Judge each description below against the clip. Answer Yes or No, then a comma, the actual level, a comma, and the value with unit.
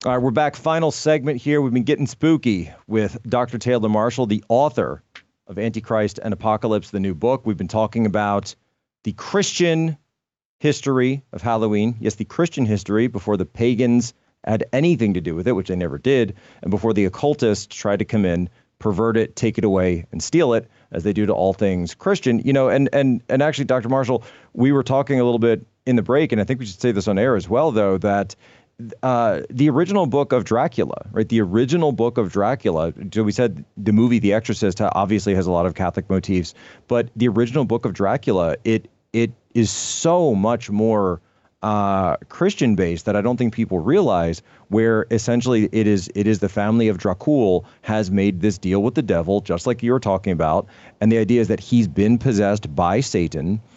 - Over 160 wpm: Yes, fast, 205 wpm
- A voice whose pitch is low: Yes, low, 110 Hz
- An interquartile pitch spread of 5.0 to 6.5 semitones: No, average, 3.6 semitones